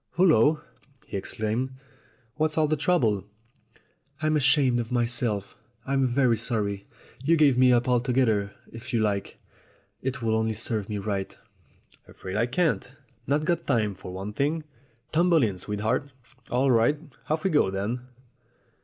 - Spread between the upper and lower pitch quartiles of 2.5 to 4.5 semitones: No, average, 5.2 semitones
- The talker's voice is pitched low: Yes, low, 120 Hz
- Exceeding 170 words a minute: No, average, 155 wpm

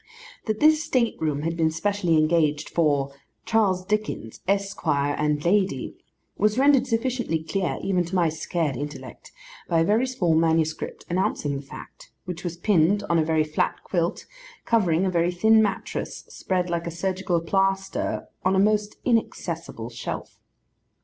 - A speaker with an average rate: Yes, average, 155 wpm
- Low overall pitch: No, medium, 175 Hz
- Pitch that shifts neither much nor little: Yes, average, 4.3 semitones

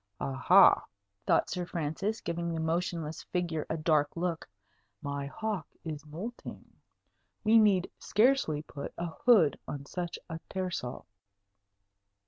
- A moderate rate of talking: No, slow, 120 wpm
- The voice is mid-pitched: Yes, medium, 170 Hz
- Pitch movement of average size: Yes, average, 3.6 semitones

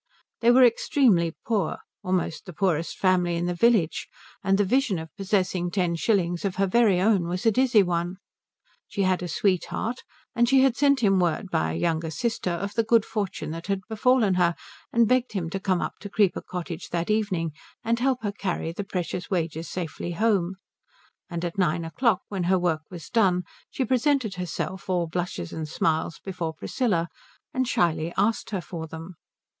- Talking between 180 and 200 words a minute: Yes, average, 185 wpm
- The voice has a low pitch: No, medium, 185 Hz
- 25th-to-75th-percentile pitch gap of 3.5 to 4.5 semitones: Yes, average, 4.2 semitones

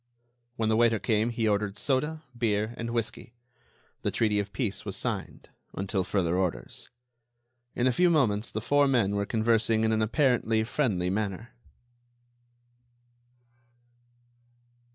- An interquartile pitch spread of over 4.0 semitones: No, narrow, 2.6 semitones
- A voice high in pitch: No, low, 110 Hz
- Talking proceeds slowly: Yes, slow, 130 wpm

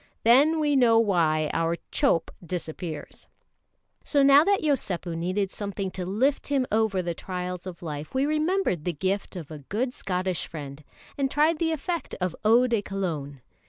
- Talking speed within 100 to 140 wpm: No, average, 165 wpm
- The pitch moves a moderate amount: No, wide, 7.9 semitones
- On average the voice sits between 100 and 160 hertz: No, high, 195 Hz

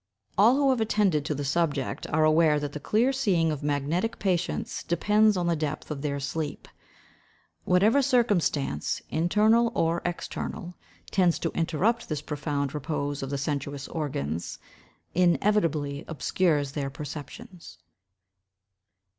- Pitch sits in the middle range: Yes, medium, 160 Hz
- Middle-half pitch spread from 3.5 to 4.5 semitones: No, wide, 5.5 semitones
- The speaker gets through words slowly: Yes, slow, 130 wpm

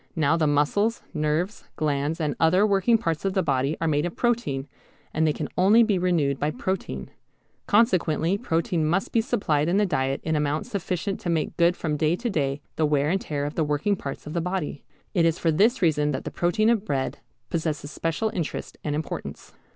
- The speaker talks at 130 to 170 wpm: No, fast, 205 wpm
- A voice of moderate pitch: Yes, medium, 165 Hz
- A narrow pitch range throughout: No, average, 4.4 semitones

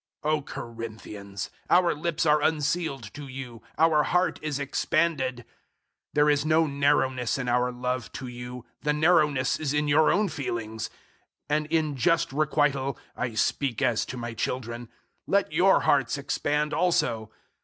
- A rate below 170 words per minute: Yes, average, 155 wpm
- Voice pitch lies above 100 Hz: Yes, medium, 140 Hz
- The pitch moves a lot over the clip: No, average, 3.9 semitones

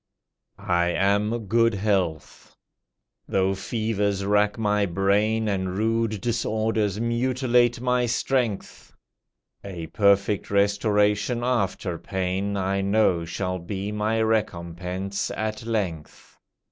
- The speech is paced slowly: Yes, slow, 100 wpm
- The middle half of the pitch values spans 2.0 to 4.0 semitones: Yes, narrow, 2.6 semitones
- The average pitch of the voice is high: No, low, 105 Hz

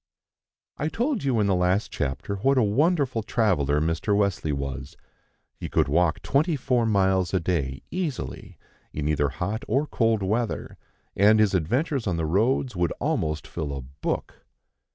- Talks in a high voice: No, low, 100 Hz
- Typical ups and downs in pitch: No, wide, 7.7 semitones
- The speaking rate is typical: Yes, average, 160 wpm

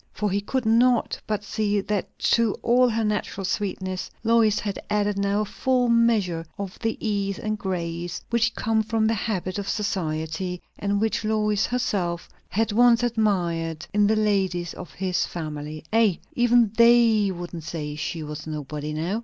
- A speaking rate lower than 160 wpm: No, average, 165 wpm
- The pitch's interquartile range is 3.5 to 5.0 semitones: Yes, average, 4.1 semitones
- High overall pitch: Yes, high, 205 Hz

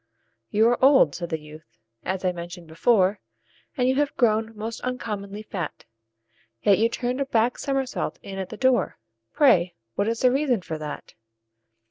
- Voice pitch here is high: Yes, high, 215 Hz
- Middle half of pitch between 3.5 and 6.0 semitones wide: Yes, wide, 5.6 semitones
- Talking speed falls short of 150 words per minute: No, average, 170 wpm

